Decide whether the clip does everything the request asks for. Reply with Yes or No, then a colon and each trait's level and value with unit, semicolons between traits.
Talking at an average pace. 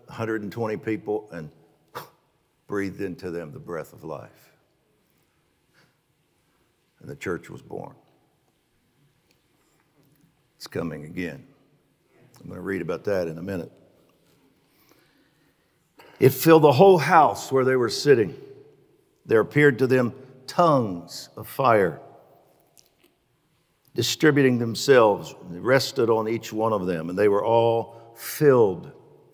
No: slow, 120 wpm